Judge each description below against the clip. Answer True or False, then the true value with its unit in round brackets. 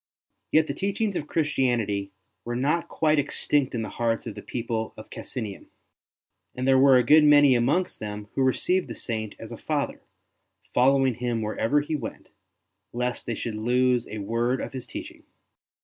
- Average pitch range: True (4.1 semitones)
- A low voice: True (125 Hz)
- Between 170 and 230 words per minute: True (175 wpm)